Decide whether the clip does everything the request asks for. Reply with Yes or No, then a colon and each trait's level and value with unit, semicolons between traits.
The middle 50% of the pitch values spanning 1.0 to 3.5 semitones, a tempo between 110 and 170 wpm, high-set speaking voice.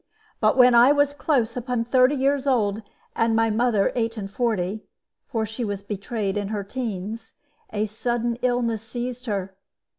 Yes: average, 2.9 semitones; average, 160 wpm; high, 230 Hz